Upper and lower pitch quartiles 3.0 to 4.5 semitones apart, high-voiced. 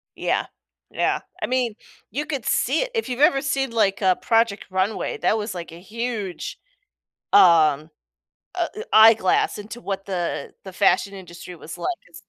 No: average, 5.2 semitones; high, 210 Hz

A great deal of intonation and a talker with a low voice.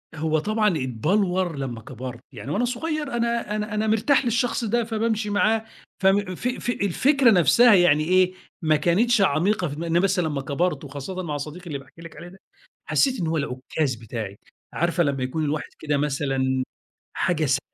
No: wide, 6.9 semitones; medium, 175 Hz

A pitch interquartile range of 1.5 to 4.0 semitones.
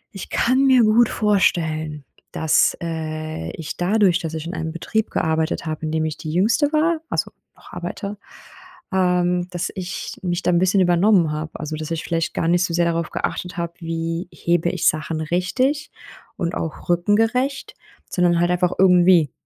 Yes: average, 2.9 semitones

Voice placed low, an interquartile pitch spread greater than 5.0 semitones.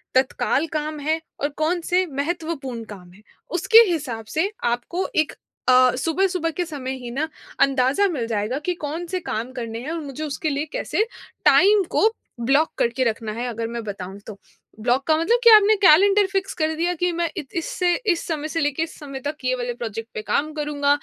No: very high, 295 Hz; wide, 5.4 semitones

